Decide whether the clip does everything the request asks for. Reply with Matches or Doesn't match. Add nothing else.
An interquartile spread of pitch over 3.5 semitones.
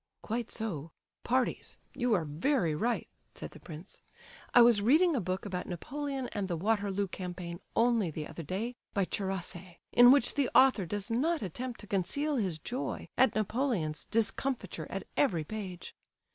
Matches